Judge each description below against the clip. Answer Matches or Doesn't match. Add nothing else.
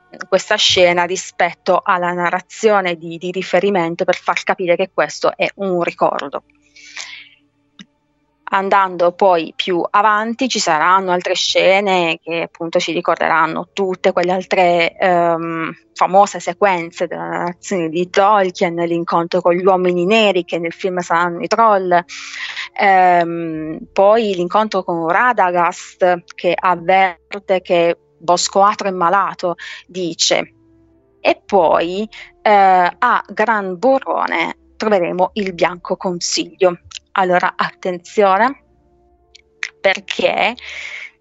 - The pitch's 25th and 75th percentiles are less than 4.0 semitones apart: Matches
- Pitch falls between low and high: Matches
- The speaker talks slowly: Matches